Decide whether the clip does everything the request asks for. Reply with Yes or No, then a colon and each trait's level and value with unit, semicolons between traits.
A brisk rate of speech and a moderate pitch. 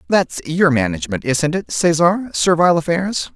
No: average, 145 wpm; medium, 160 Hz